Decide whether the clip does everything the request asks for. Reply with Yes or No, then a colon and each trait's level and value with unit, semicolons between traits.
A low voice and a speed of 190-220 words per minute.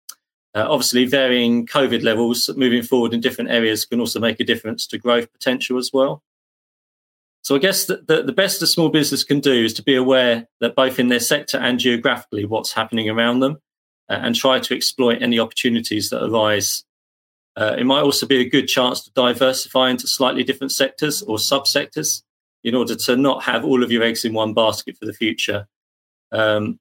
Yes: low, 120 Hz; average, 195 wpm